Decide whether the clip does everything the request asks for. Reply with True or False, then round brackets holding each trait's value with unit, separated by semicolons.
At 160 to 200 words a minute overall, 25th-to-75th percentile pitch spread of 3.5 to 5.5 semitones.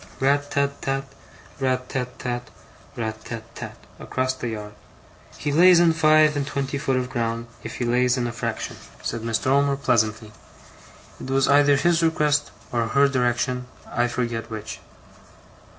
False (165 wpm; 3.0 semitones)